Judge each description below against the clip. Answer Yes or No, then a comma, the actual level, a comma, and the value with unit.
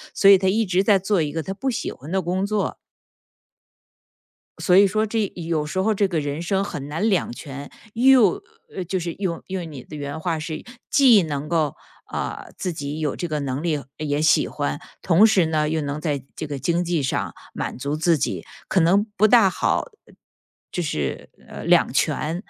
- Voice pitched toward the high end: No, medium, 170 Hz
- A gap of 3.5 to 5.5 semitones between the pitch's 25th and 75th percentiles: Yes, average, 4.4 semitones